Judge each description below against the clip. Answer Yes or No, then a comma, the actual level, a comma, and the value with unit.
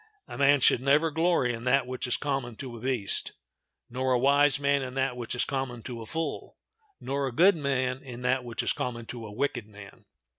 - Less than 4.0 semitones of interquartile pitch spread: Yes, narrow, 2.5 semitones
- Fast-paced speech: Yes, fast, 220 wpm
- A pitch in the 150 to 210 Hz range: No, low, 130 Hz